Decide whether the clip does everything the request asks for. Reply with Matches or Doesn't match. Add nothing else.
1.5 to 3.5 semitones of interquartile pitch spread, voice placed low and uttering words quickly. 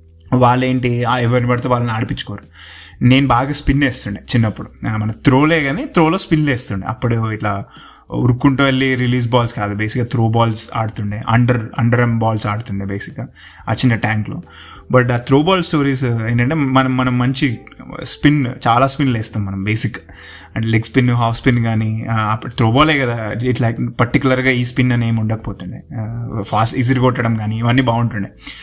Matches